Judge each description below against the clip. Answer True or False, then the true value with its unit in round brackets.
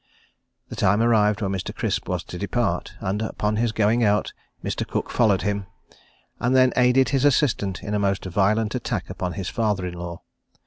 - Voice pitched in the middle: False (105 Hz)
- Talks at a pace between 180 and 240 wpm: True (185 wpm)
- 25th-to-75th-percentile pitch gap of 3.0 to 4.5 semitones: True (3.4 semitones)